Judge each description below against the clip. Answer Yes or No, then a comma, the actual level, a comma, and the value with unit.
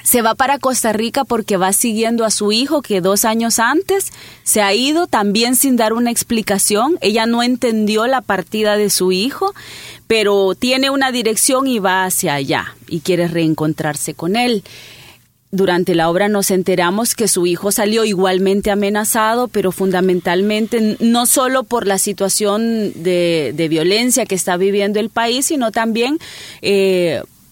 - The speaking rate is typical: Yes, average, 160 wpm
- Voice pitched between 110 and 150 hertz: No, high, 210 Hz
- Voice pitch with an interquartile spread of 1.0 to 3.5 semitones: No, average, 3.9 semitones